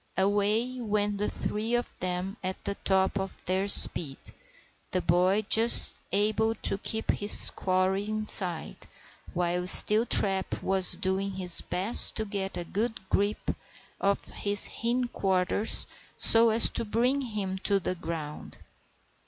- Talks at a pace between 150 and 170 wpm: No, slow, 135 wpm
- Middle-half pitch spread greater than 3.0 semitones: No, narrow, 2.6 semitones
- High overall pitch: Yes, high, 200 Hz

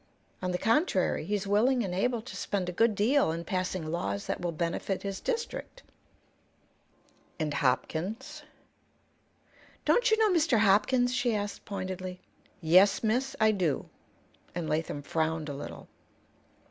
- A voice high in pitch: Yes, high, 195 Hz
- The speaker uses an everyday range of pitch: No, wide, 6.2 semitones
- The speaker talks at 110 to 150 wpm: Yes, average, 140 wpm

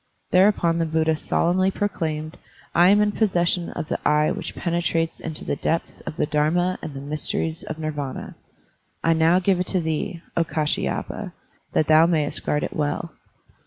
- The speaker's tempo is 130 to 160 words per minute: No, average, 170 wpm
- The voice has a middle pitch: Yes, medium, 165 Hz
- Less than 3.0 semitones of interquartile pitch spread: Yes, narrow, 2.4 semitones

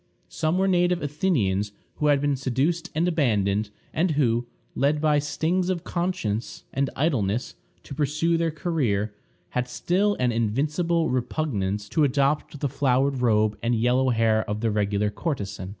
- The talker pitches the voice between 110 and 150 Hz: Yes, low, 135 Hz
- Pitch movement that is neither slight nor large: No, wide, 6.3 semitones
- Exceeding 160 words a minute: No, average, 150 wpm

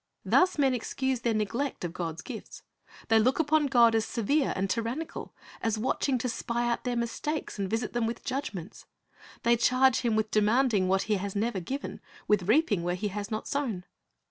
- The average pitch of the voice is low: No, high, 230 Hz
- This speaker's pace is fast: No, average, 190 wpm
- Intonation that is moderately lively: Yes, average, 4.0 semitones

